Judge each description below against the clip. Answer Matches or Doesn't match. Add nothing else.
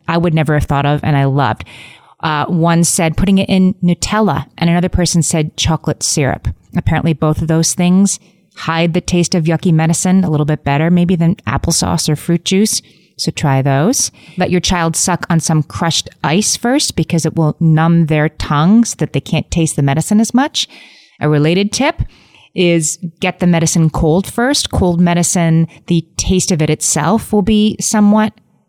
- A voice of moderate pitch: Matches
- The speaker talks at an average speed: Matches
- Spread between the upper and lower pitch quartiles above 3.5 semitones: Doesn't match